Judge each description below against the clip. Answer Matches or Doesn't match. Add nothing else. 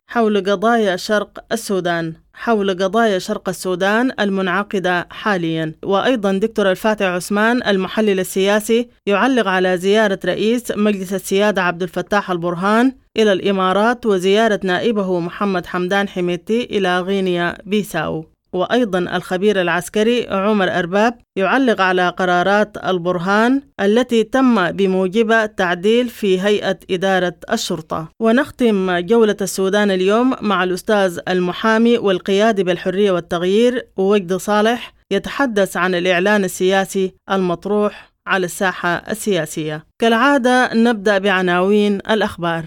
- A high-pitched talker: Matches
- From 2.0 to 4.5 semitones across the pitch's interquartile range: Matches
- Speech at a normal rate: Doesn't match